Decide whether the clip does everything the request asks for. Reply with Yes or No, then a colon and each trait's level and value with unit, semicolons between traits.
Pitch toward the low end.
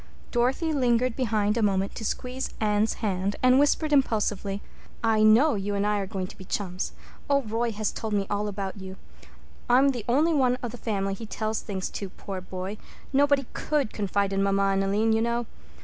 No: high, 215 Hz